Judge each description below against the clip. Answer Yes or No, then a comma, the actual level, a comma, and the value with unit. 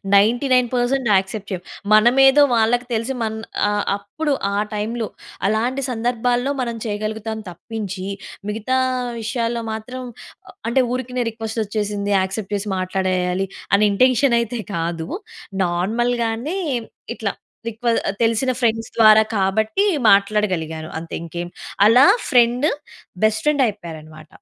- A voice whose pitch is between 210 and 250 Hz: Yes, high, 220 Hz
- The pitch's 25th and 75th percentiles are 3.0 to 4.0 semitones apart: Yes, average, 3.5 semitones